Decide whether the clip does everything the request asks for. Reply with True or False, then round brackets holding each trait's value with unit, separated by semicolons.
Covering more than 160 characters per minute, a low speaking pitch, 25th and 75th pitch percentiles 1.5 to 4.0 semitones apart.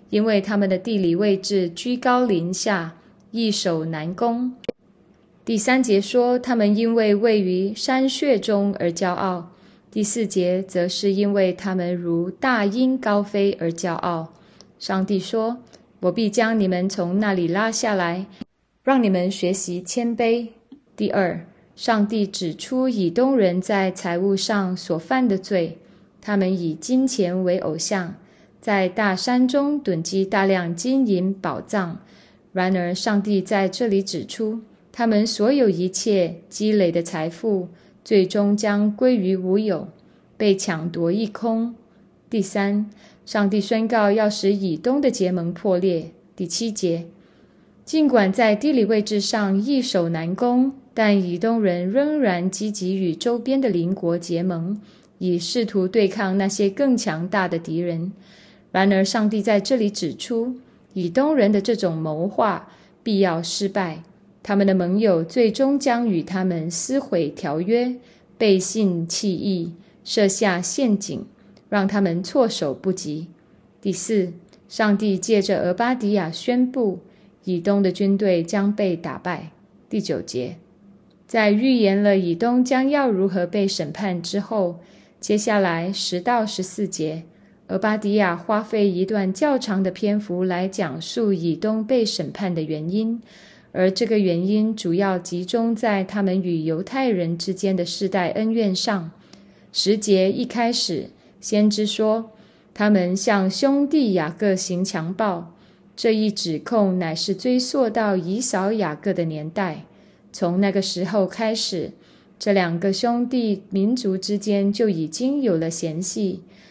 False (205 characters per minute; 200 Hz; 3.3 semitones)